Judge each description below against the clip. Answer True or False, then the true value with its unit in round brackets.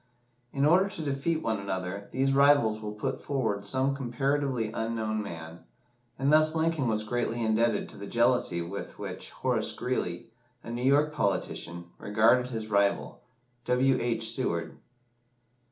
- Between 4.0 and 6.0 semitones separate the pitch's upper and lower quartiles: True (4.5 semitones)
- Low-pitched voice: True (120 Hz)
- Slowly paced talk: False (145 wpm)